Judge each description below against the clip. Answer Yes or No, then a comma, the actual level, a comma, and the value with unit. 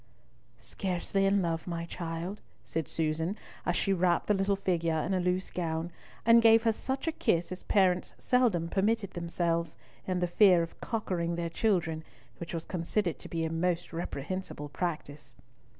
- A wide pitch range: No, average, 2.8 semitones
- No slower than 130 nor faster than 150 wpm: No, average, 165 wpm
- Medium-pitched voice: Yes, medium, 175 Hz